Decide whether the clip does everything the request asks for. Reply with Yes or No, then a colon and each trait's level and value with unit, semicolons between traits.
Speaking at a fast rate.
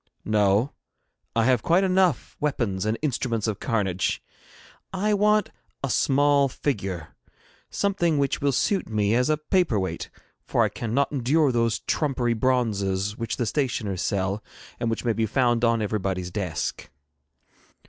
No: average, 145 wpm